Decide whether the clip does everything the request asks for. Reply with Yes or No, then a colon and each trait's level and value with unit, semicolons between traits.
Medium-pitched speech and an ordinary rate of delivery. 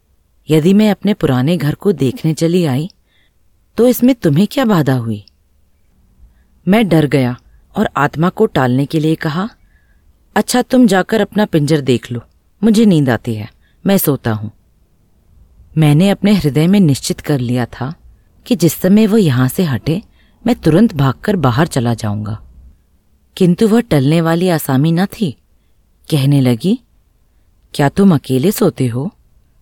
Yes: medium, 150 Hz; average, 150 wpm